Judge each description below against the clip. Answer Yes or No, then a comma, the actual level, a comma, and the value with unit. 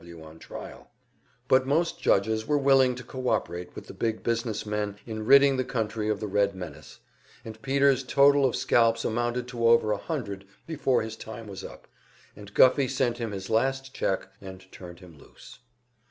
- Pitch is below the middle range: Yes, low, 115 Hz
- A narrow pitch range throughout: No, average, 4.3 semitones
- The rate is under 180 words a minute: No, average, 185 wpm